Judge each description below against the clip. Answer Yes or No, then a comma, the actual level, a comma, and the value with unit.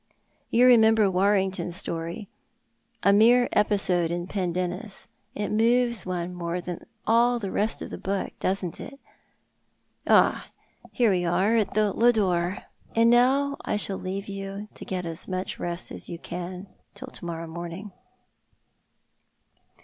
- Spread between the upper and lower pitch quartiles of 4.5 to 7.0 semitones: No, average, 3.9 semitones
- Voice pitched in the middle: No, high, 195 Hz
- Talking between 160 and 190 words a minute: No, average, 145 wpm